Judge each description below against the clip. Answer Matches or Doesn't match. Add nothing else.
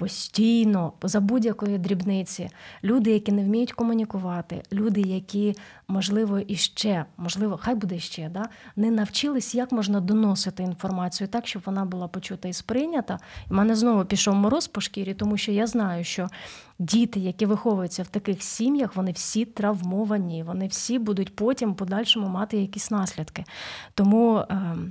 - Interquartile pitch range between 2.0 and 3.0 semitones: Matches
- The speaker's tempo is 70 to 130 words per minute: Doesn't match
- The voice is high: Matches